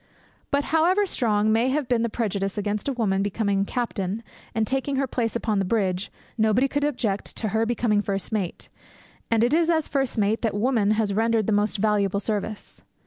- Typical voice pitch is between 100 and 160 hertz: No, high, 220 Hz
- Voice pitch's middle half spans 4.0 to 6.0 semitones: No, average, 3.3 semitones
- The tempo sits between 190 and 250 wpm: Yes, average, 195 wpm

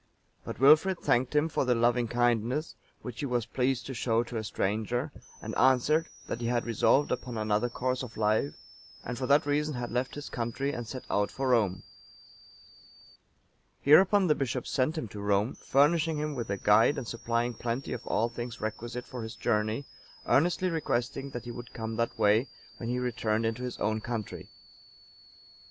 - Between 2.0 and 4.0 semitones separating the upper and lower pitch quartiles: Yes, average, 3.2 semitones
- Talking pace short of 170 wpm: No, average, 180 wpm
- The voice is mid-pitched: No, low, 120 Hz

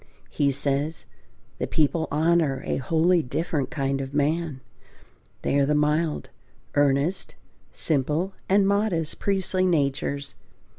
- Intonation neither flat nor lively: Yes, average, 3.4 semitones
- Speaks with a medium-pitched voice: Yes, medium, 150 Hz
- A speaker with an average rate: No, slow, 115 wpm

